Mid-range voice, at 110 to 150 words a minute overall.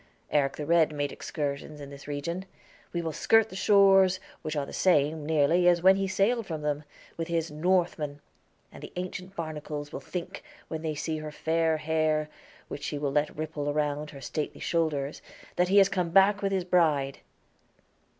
No: medium, 160 Hz; average, 185 wpm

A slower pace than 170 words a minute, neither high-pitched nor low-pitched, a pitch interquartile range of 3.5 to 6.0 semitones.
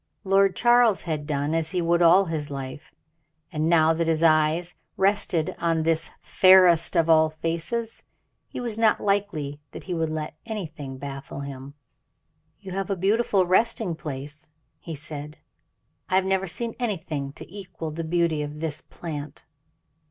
Yes: average, 160 wpm; medium, 165 Hz; average, 3.8 semitones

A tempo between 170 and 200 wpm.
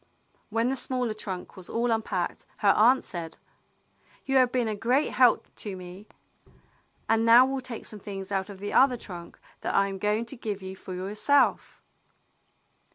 Yes: average, 175 wpm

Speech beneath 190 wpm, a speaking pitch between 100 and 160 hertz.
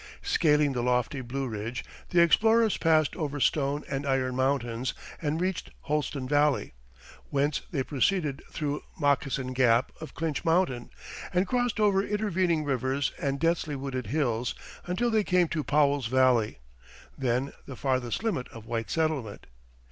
Yes: average, 145 wpm; medium, 140 Hz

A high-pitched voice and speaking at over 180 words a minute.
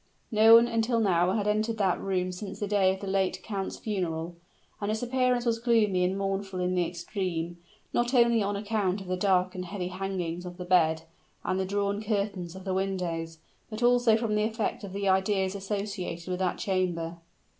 Yes: high, 195 Hz; average, 195 wpm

